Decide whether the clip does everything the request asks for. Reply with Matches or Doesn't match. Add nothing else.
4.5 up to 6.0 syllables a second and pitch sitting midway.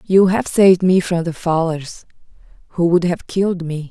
Matches